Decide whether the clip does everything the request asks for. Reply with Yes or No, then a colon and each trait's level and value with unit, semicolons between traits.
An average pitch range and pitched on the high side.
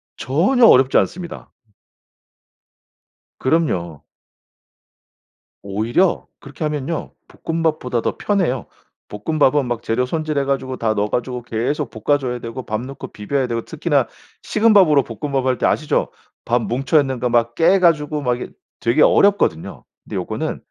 No: average, 4.6 semitones; low, 130 Hz